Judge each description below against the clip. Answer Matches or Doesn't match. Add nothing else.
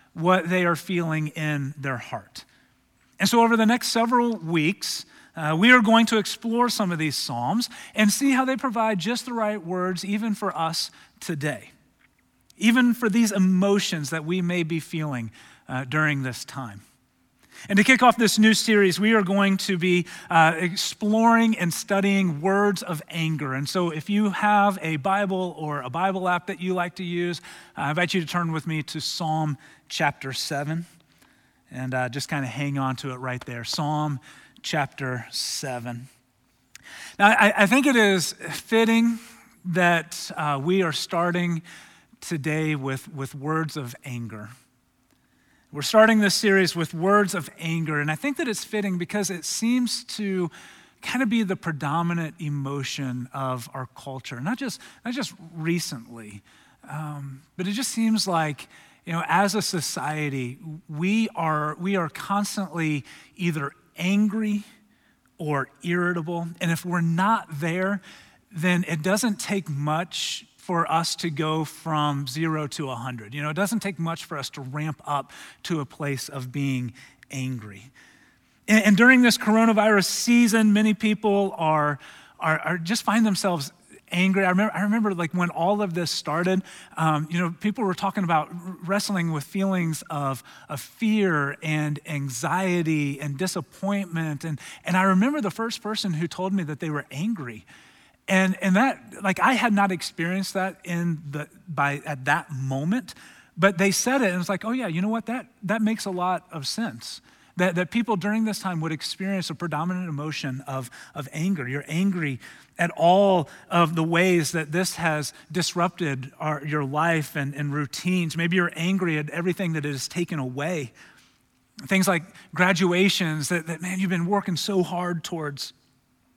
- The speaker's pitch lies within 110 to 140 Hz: Doesn't match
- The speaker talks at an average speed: Matches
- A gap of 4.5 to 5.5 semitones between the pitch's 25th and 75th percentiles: Matches